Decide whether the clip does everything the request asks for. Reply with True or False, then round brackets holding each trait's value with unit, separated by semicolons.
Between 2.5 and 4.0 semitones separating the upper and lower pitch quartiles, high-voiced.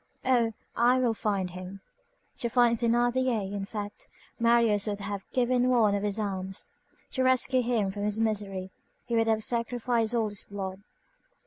True (3.0 semitones; 220 Hz)